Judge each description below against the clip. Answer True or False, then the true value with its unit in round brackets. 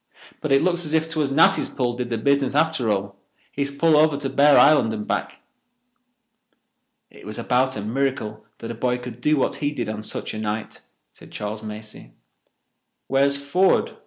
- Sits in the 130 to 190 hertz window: True (135 Hz)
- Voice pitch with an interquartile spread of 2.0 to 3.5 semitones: False (5.1 semitones)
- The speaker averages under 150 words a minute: False (180 wpm)